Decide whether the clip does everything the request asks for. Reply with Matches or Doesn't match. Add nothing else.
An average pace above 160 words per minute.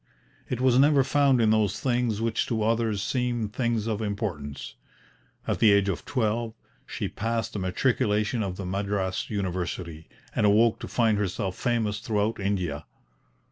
Doesn't match